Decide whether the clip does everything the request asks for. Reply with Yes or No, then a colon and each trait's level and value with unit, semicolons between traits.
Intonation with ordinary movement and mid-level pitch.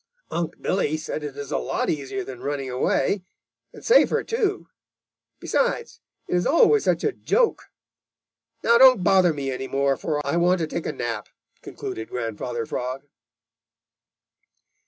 No: wide, 5.9 semitones; medium, 150 Hz